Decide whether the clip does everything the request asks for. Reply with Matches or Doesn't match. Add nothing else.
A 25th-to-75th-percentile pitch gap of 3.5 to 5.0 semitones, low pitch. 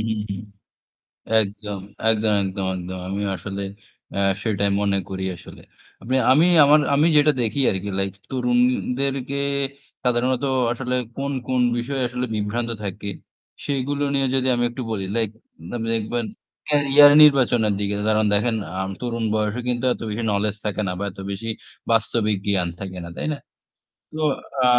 Matches